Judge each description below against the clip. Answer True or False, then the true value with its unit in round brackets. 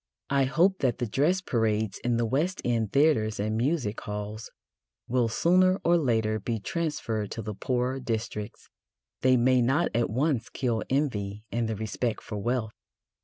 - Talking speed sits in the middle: True (165 wpm)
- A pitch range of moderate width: True (4.0 semitones)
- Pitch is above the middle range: False (120 Hz)